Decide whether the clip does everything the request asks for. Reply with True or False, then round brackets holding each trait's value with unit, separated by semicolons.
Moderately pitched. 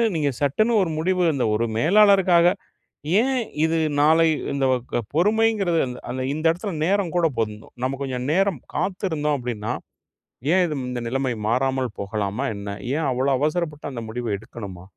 True (150 Hz)